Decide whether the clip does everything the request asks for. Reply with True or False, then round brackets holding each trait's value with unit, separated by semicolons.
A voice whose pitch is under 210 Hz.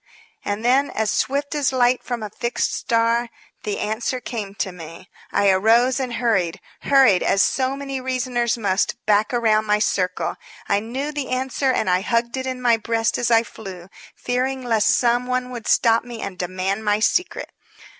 False (235 Hz)